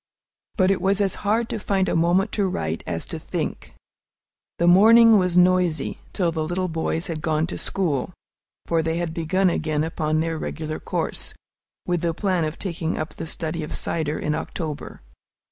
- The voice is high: No, medium, 170 Hz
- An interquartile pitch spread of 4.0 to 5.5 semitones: No, average, 3.0 semitones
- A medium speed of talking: Yes, average, 180 wpm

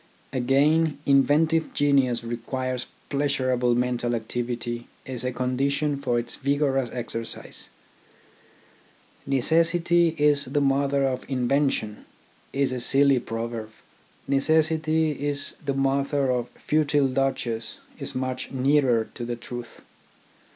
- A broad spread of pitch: No, average, 2.9 semitones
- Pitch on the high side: No, low, 135 Hz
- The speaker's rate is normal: No, slow, 115 wpm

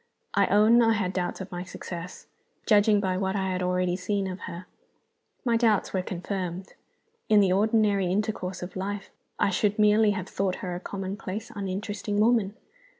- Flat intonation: Yes, narrow, 2.2 semitones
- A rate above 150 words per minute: Yes, average, 170 wpm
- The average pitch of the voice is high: Yes, high, 195 Hz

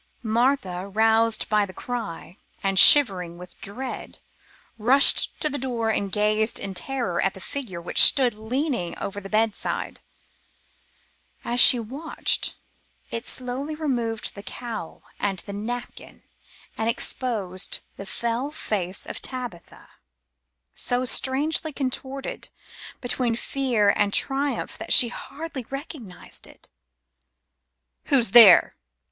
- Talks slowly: Yes, slow, 120 wpm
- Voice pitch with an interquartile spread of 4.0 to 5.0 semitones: Yes, average, 4.6 semitones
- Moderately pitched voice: No, high, 230 Hz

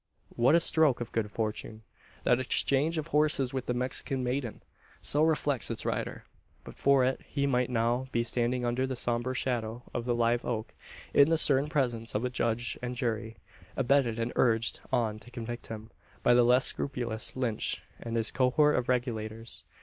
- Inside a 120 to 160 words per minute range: No, average, 180 wpm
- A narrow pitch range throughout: Yes, narrow, 2.3 semitones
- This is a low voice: Yes, low, 125 Hz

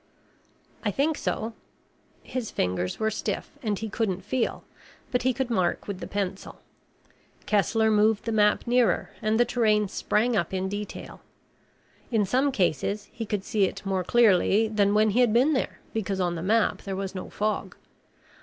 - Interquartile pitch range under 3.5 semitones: Yes, average, 2.8 semitones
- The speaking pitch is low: No, high, 210 Hz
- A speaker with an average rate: Yes, average, 175 wpm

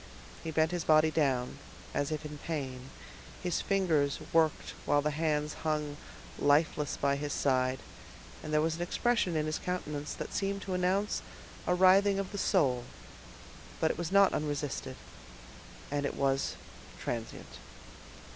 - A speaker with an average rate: Yes, average, 150 wpm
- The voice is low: No, medium, 155 Hz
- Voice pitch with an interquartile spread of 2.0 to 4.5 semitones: Yes, average, 3.8 semitones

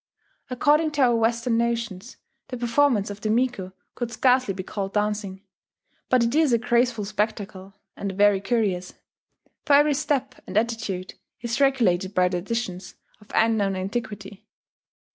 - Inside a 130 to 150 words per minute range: Yes, average, 145 wpm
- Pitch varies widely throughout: No, average, 3.8 semitones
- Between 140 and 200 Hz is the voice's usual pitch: No, high, 225 Hz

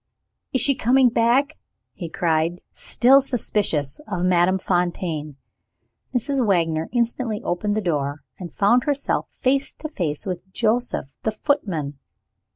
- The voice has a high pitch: Yes, high, 200 Hz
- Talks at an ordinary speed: No, slow, 130 wpm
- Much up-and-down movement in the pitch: Yes, wide, 6.6 semitones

